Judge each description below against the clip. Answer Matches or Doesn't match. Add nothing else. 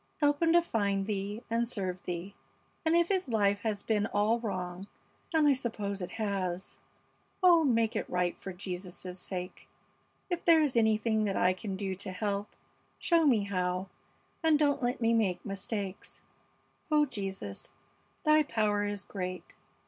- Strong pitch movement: Doesn't match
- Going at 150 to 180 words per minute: Matches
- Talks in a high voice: Matches